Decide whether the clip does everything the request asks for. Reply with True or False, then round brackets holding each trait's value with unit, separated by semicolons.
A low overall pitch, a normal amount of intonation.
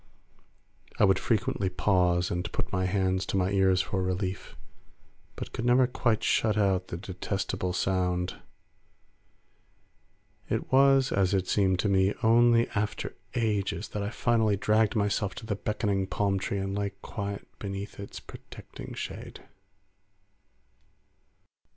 False (100 Hz; 2.3 semitones)